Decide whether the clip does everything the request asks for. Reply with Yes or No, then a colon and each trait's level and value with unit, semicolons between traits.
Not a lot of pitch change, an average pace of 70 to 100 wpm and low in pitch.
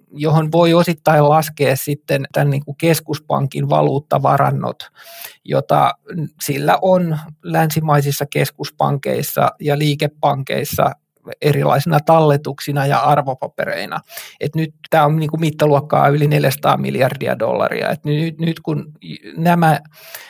No: narrow, 1.9 semitones; slow, 95 wpm; medium, 150 Hz